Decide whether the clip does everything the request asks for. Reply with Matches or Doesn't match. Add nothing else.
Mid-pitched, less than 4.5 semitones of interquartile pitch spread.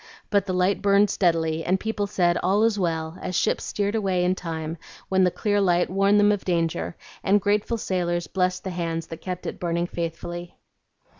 Matches